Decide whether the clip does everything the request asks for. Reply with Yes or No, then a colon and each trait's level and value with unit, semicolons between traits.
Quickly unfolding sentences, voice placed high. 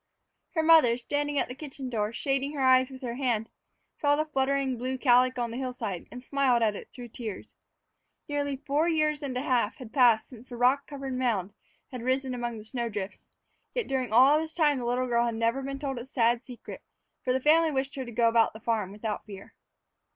Yes: fast, 215 wpm; very high, 255 Hz